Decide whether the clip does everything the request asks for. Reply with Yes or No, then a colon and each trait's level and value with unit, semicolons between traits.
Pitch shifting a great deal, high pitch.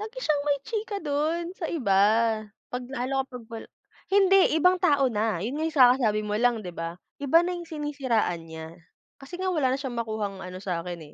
Yes: wide, 7.5 semitones; very high, 265 Hz